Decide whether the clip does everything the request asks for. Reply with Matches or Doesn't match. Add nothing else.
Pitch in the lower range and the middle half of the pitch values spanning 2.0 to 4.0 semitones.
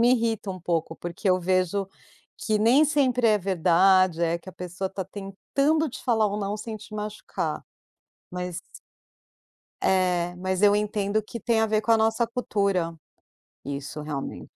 Doesn't match